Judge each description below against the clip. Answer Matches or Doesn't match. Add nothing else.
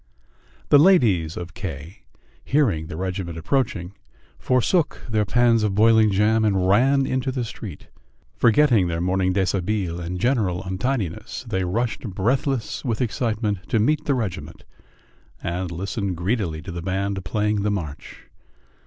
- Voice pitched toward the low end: Matches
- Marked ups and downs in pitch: Doesn't match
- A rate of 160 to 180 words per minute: Doesn't match